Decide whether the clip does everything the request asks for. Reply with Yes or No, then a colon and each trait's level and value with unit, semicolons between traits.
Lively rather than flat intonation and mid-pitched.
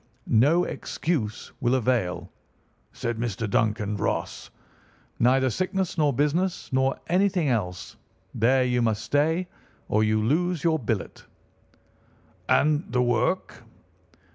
No: wide, 6.3 semitones; low, 130 Hz